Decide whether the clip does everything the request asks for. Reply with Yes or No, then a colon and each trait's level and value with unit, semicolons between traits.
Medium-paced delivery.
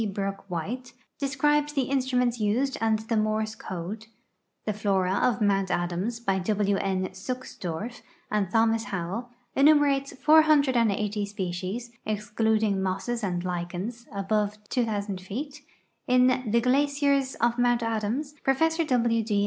No: slow, 125 wpm